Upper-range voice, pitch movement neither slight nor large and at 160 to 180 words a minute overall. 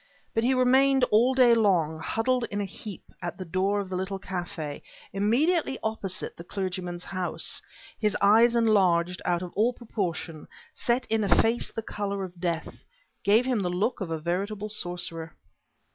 Yes: high, 200 Hz; average, 4.2 semitones; average, 170 wpm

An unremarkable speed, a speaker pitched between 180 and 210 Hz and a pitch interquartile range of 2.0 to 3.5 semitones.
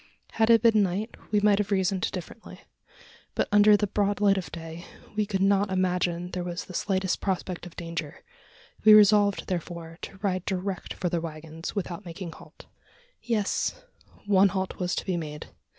Yes: average, 175 wpm; high, 190 Hz; average, 2.8 semitones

